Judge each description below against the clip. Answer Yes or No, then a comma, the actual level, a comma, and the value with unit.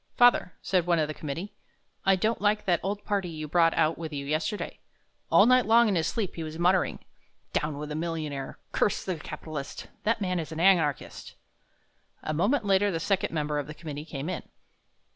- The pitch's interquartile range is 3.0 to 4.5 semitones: Yes, average, 4.2 semitones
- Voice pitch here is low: No, medium, 170 Hz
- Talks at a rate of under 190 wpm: No, average, 200 wpm